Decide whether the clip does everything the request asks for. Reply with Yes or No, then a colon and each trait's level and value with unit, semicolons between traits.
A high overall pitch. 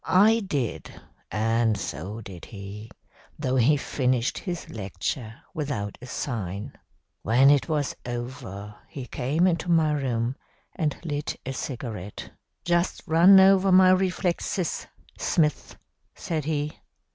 No: low, 135 Hz